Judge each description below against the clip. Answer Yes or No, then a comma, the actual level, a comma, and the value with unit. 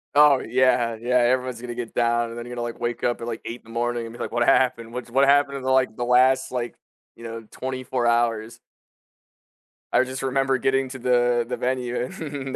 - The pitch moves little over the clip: Yes, narrow, 1.8 semitones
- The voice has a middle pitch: No, low, 125 Hz